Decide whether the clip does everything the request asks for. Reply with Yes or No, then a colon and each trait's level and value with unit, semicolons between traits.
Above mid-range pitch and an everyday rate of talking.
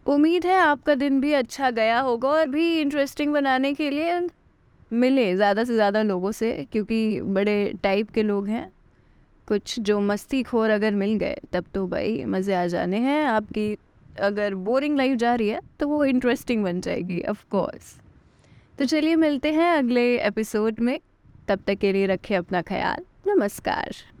Yes: high, 230 Hz; average, 170 wpm